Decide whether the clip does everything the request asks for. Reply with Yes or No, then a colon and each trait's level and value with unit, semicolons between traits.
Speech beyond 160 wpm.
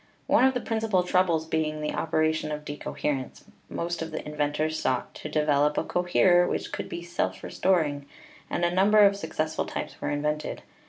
Yes: average, 190 wpm